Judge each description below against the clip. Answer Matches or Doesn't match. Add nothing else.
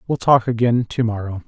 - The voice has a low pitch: Matches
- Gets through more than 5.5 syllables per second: Doesn't match